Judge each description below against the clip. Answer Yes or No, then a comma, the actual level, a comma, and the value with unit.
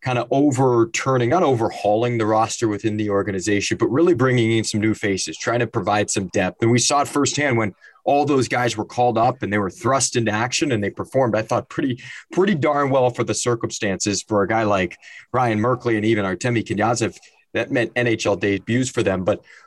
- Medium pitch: No, low, 115 Hz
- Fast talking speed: Yes, fast, 210 wpm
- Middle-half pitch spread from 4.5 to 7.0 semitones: No, average, 3.2 semitones